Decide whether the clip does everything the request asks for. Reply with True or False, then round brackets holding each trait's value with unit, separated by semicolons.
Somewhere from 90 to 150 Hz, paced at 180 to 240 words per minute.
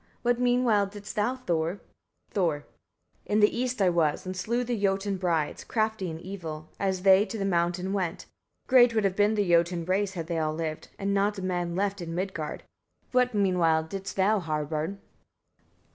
False (190 Hz; 185 wpm)